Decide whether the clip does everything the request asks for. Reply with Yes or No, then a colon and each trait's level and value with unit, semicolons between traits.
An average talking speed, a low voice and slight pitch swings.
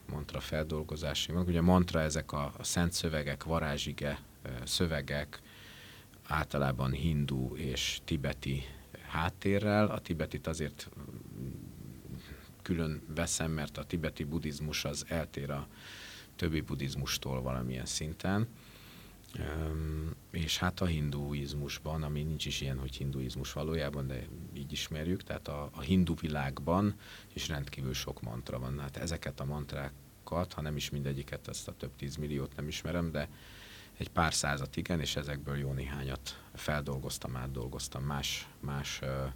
No: average, 135 wpm; very low, 75 Hz; average, 3.2 semitones